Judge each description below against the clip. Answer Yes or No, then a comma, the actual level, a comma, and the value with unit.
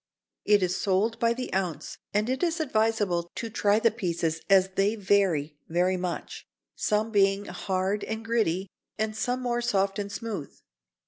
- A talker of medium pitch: No, high, 200 Hz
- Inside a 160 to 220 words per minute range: Yes, average, 165 wpm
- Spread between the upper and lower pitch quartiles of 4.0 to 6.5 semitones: No, average, 3.3 semitones